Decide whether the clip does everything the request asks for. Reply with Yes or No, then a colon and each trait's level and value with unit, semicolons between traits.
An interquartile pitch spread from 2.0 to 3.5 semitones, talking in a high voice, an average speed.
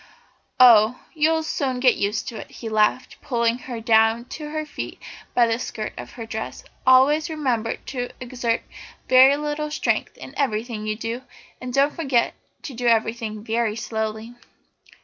Yes: average, 3.2 semitones; high, 240 Hz; average, 165 wpm